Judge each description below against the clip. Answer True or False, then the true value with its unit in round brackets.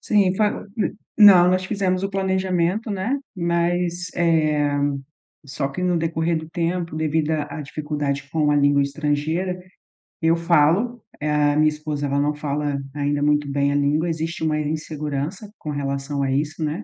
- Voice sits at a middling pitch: True (155 Hz)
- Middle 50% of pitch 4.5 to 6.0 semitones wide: False (3.4 semitones)